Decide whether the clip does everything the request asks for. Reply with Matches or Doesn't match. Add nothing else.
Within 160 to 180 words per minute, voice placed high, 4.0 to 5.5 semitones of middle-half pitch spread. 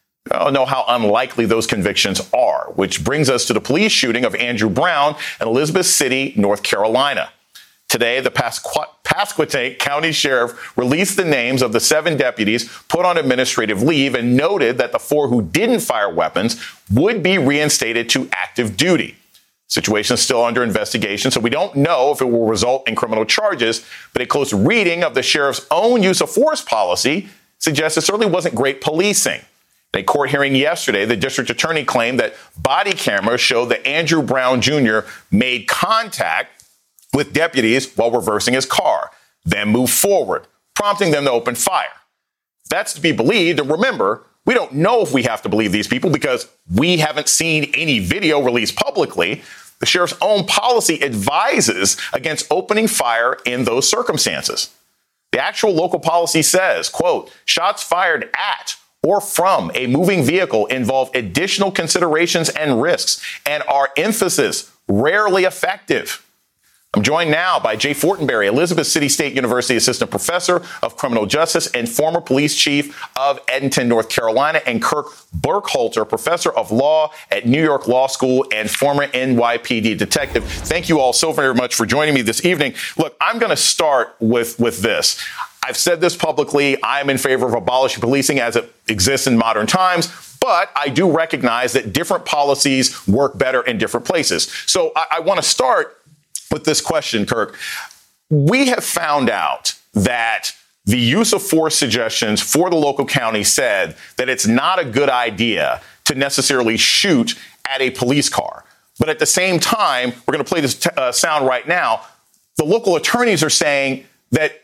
Doesn't match